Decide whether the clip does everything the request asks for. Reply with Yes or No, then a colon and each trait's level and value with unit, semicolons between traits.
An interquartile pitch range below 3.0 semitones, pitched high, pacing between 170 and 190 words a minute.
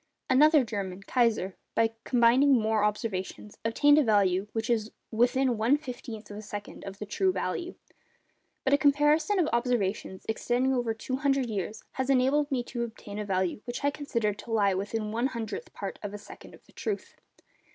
No: average, 4.2 semitones; high, 230 Hz; average, 180 wpm